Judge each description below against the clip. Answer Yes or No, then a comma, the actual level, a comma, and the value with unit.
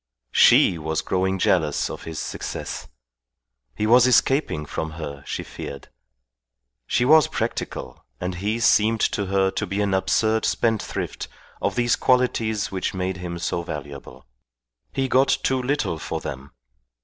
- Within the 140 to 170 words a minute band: Yes, average, 145 wpm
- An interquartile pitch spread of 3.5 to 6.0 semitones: Yes, wide, 5.6 semitones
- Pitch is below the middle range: Yes, low, 100 Hz